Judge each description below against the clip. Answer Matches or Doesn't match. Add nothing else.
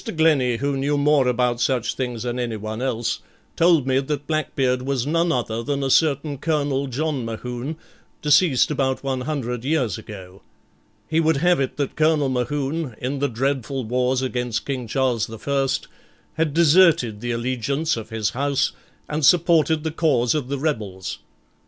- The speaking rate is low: Doesn't match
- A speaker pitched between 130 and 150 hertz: Matches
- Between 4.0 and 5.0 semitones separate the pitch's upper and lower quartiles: Doesn't match